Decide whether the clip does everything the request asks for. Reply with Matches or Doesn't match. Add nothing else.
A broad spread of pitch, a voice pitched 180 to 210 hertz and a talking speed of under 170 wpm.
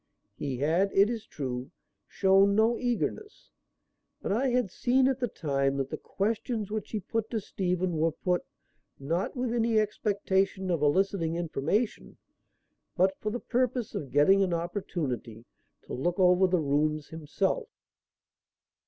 Matches